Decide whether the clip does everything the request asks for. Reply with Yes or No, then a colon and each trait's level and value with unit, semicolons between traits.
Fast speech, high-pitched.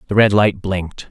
No: fast, 215 wpm; low, 100 Hz